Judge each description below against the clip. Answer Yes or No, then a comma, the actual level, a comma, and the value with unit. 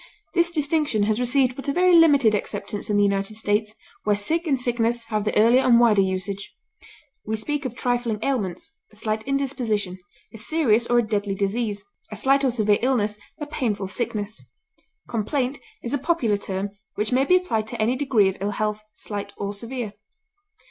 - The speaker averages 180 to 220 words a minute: Yes, average, 185 wpm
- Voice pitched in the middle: No, high, 225 Hz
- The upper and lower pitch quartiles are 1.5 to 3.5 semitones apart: No, average, 4.3 semitones